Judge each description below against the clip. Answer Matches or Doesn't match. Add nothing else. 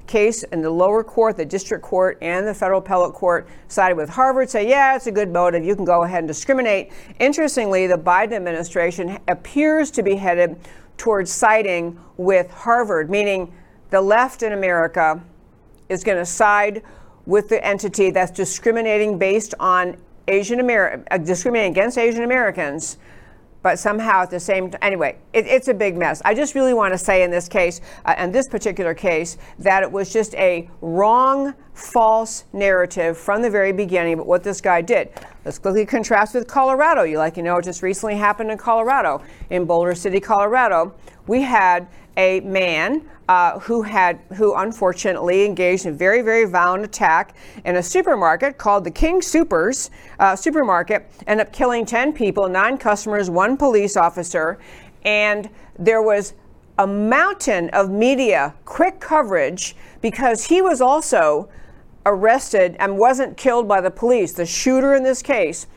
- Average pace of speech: Matches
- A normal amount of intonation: Matches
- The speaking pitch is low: Doesn't match